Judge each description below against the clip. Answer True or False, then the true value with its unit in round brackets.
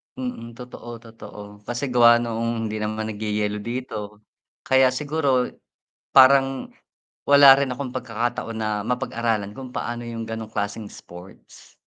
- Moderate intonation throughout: True (3.0 semitones)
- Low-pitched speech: True (115 Hz)